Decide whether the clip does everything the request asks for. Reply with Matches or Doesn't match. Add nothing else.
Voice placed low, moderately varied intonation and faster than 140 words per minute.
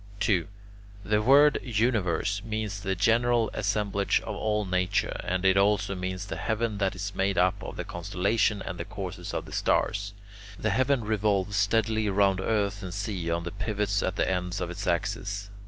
Doesn't match